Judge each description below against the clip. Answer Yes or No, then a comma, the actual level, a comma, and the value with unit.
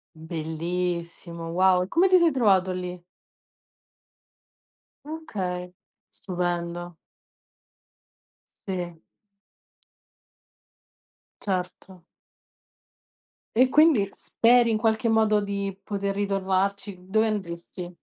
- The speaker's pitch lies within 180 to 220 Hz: Yes, high, 190 Hz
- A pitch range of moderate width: Yes, average, 3.4 semitones